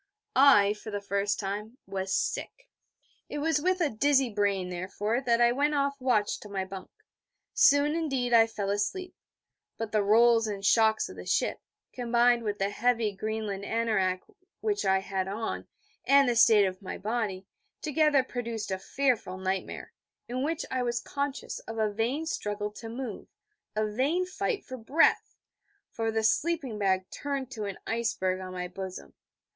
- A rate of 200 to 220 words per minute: No, average, 170 wpm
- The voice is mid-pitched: No, high, 225 Hz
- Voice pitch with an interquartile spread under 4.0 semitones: No, average, 4.7 semitones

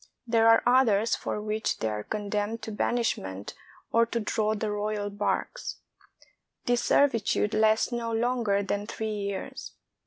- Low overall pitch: No, high, 215 Hz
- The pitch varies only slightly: Yes, narrow, 2.0 semitones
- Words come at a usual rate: Yes, average, 145 wpm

